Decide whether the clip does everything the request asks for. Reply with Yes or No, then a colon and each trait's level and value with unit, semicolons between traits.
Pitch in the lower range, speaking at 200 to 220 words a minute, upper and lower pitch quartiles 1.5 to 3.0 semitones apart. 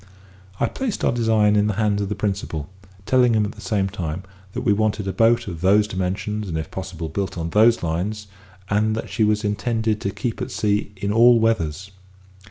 Yes: low, 105 Hz; fast, 205 wpm; narrow, 2.5 semitones